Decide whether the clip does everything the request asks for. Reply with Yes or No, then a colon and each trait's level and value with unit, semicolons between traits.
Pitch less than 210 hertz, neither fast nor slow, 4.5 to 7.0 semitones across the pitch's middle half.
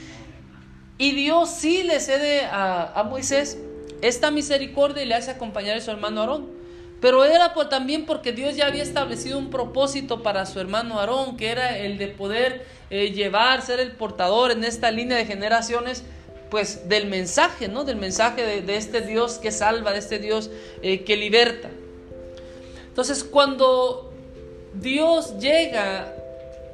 No: high, 235 Hz; average, 155 wpm; wide, 5.5 semitones